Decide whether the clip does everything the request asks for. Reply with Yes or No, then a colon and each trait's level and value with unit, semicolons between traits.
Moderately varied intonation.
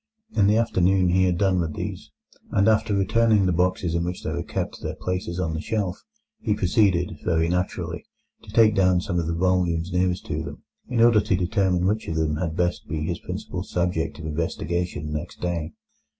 No: narrow, 2.3 semitones